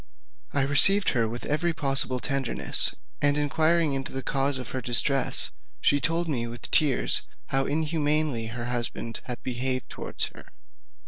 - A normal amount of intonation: Yes, average, 3.3 semitones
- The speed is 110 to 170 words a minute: Yes, average, 150 wpm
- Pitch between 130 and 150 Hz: Yes, low, 135 Hz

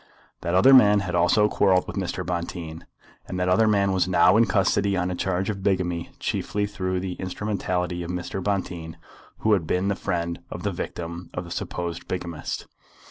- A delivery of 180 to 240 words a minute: Yes, average, 190 wpm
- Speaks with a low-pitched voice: Yes, very low, 90 Hz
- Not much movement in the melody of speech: Yes, narrow, 2.2 semitones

